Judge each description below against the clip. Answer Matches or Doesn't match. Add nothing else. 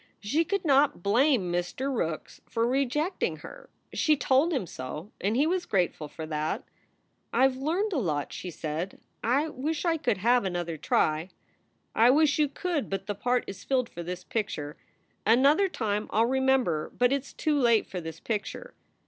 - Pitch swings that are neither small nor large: Doesn't match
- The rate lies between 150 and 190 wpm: Matches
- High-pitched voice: Matches